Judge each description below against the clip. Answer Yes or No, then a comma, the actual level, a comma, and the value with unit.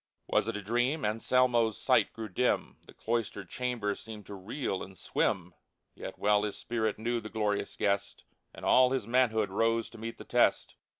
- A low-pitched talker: Yes, low, 110 Hz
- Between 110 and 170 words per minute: No, average, 180 wpm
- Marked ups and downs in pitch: No, narrow, 2.6 semitones